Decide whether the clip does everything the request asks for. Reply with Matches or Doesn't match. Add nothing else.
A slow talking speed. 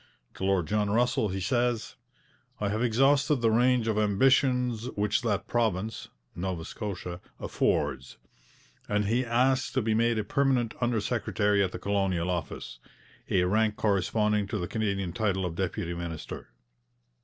Doesn't match